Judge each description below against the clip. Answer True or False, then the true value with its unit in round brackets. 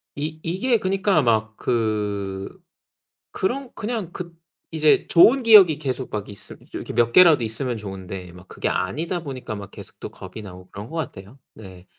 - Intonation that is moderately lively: False (9.0 semitones)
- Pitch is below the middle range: True (125 Hz)